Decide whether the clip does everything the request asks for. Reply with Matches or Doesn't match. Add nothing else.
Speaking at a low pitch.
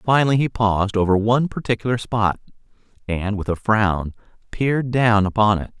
Matches